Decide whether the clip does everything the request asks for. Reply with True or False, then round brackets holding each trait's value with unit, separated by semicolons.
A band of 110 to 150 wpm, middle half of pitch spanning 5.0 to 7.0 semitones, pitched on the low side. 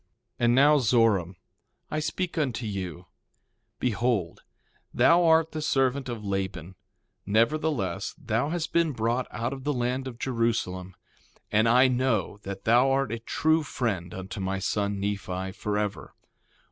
True (145 wpm; 5.4 semitones; 115 Hz)